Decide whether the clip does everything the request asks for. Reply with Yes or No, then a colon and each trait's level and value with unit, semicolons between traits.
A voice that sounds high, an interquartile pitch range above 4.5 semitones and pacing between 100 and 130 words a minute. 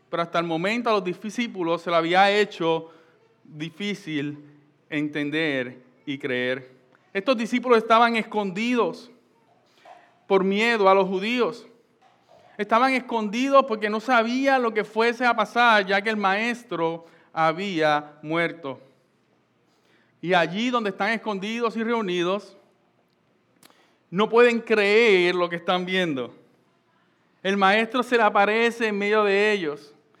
Yes: high, 195 Hz; wide, 5.4 semitones; slow, 125 wpm